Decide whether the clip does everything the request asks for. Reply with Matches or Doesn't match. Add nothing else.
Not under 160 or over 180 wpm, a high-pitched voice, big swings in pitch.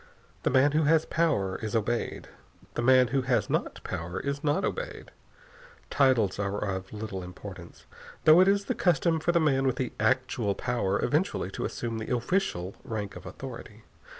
Doesn't match